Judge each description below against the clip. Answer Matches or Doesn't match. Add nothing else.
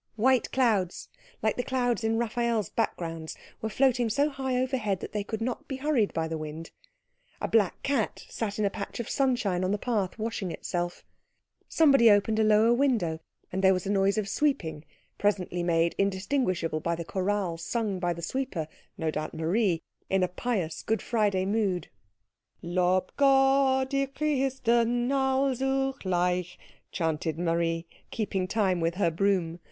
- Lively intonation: Matches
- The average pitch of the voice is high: Matches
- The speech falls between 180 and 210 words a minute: Doesn't match